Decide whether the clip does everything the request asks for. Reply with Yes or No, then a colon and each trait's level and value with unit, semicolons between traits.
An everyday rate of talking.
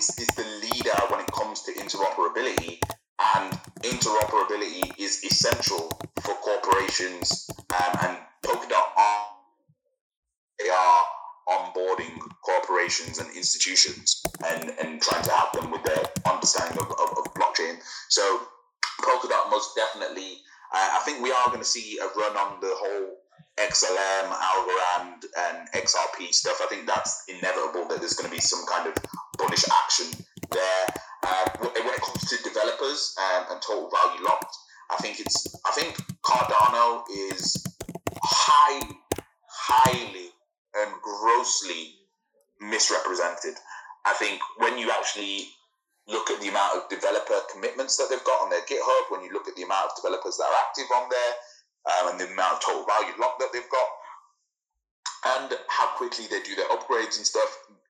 Yes: average, 155 wpm